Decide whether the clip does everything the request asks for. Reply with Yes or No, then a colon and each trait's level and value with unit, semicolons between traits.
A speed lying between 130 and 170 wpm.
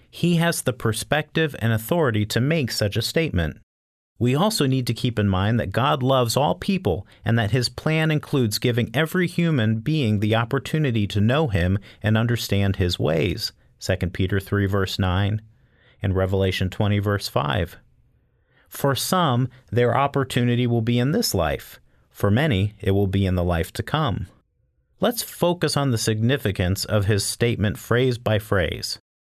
Yes: average, 165 wpm